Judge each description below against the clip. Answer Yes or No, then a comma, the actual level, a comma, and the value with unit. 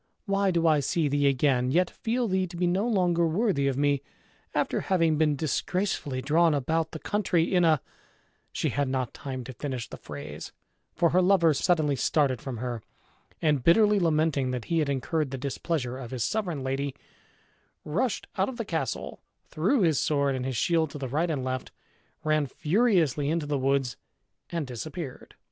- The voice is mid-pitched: Yes, medium, 155 Hz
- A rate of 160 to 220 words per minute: Yes, average, 185 wpm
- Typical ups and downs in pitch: Yes, average, 4.5 semitones